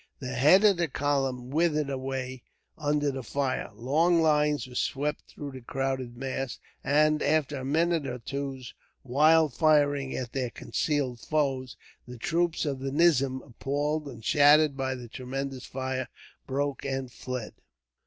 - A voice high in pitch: No, low, 135 Hz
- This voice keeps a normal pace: Yes, average, 150 wpm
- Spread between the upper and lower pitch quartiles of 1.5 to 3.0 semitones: Yes, narrow, 2.4 semitones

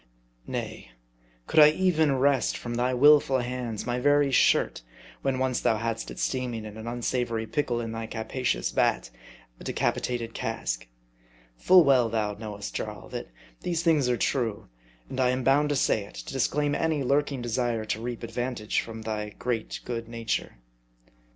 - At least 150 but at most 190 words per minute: Yes, average, 170 wpm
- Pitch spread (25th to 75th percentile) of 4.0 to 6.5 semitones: No, average, 3.2 semitones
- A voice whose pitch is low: Yes, low, 120 Hz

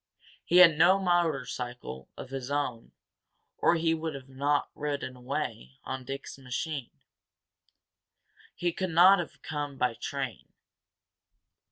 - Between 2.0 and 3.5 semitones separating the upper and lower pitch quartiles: No, average, 4.2 semitones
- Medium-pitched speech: Yes, medium, 145 Hz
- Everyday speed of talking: No, slow, 125 wpm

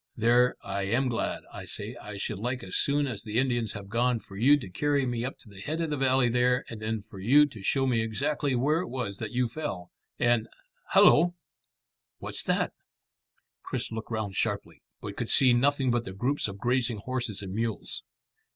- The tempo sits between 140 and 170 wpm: No, fast, 205 wpm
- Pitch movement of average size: Yes, average, 3.7 semitones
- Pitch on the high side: No, low, 120 Hz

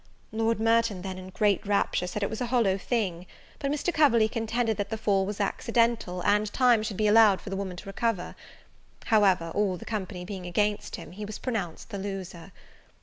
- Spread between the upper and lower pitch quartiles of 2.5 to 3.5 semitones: Yes, average, 3.0 semitones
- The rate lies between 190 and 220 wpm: Yes, average, 200 wpm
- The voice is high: Yes, high, 205 Hz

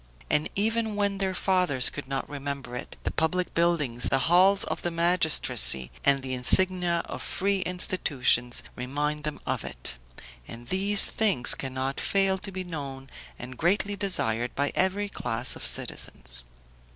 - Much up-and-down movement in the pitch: Yes, wide, 6.5 semitones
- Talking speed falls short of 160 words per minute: Yes, average, 150 wpm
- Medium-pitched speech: Yes, medium, 160 Hz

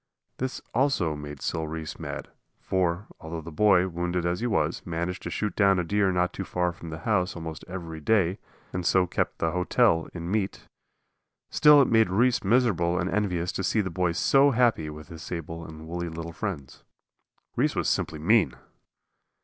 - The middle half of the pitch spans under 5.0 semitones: Yes, average, 3.9 semitones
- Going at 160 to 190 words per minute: Yes, average, 185 wpm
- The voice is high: No, very low, 90 Hz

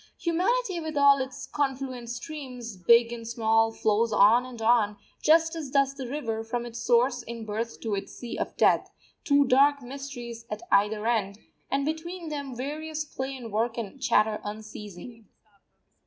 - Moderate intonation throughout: Yes, average, 4.0 semitones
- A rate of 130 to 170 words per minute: Yes, average, 165 wpm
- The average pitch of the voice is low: No, high, 245 Hz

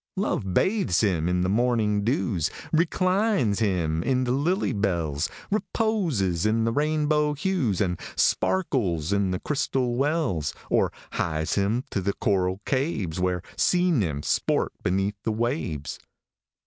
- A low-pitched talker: Yes, low, 110 Hz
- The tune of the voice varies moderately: No, wide, 8.4 semitones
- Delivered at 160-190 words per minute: No, slow, 135 wpm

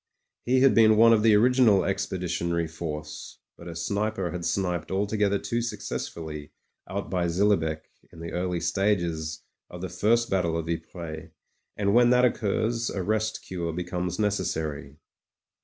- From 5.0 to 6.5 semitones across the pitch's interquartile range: No, average, 4.1 semitones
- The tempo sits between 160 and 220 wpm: No, average, 150 wpm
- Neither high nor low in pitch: No, very low, 95 Hz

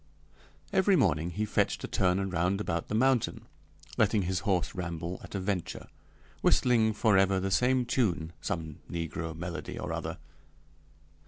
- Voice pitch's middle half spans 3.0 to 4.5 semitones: Yes, average, 4.0 semitones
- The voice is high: No, very low, 95 Hz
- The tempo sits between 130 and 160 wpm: Yes, average, 145 wpm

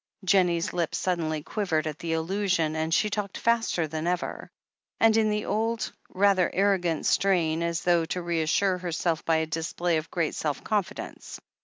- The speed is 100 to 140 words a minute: No, average, 170 wpm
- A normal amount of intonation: Yes, average, 3.5 semitones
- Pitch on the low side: No, medium, 175 Hz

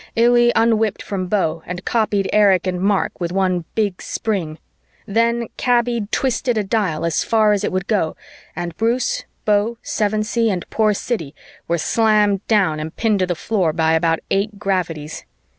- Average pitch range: Yes, average, 4.0 semitones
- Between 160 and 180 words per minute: Yes, average, 170 wpm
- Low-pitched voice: No, high, 205 Hz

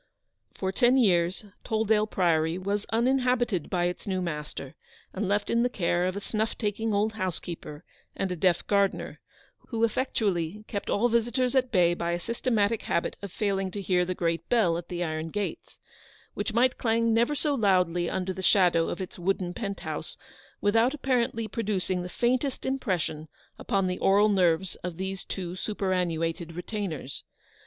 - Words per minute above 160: Yes, average, 170 wpm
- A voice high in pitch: Yes, high, 195 Hz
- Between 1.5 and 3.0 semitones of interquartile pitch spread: No, average, 4.1 semitones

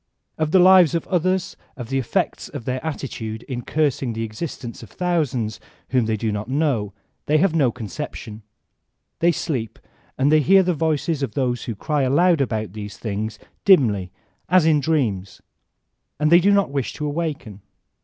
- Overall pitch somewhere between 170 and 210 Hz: No, low, 135 Hz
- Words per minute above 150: Yes, average, 175 wpm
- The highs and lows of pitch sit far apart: Yes, wide, 6.3 semitones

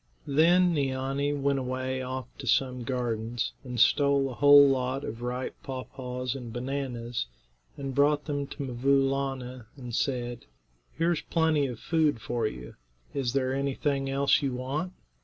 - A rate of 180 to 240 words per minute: No, average, 155 wpm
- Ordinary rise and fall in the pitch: No, narrow, 2.1 semitones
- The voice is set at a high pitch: No, low, 135 Hz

